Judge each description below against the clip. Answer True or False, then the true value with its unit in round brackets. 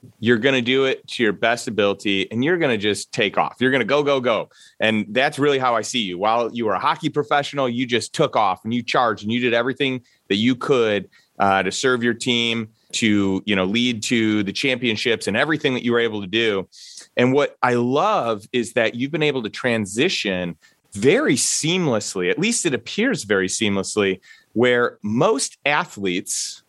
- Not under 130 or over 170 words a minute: False (205 wpm)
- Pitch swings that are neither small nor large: True (3.7 semitones)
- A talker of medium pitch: False (120 Hz)